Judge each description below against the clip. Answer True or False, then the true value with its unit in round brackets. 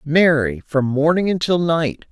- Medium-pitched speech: True (155 Hz)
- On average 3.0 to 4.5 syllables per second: True (4.0 syllables/s)